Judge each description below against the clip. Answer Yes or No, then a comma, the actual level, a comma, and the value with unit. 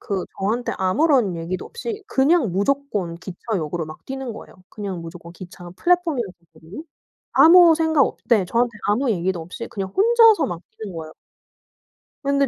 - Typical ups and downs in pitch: No, wide, 8.0 semitones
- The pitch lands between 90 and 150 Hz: No, high, 210 Hz